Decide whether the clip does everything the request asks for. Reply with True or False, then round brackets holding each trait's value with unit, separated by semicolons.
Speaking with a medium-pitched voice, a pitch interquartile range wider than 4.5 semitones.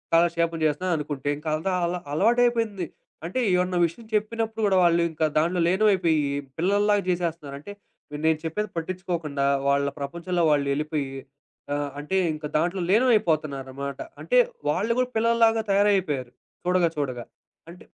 True (170 Hz; 5.0 semitones)